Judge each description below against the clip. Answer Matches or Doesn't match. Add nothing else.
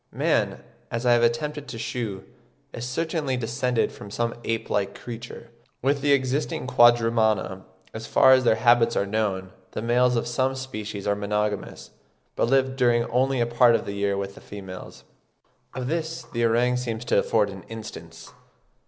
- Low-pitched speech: Matches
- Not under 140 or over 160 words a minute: Doesn't match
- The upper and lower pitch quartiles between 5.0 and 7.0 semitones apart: Doesn't match